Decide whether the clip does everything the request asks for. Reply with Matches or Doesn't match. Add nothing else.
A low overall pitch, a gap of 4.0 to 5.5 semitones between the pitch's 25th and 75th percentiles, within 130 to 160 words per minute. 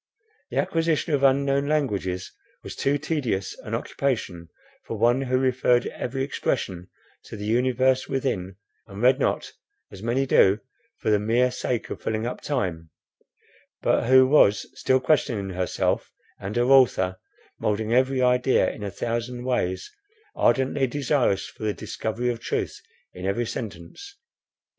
Matches